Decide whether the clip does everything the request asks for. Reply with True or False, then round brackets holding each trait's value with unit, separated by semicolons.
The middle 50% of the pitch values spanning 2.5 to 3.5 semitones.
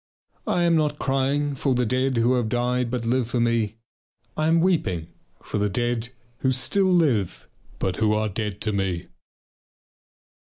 False (4.1 semitones)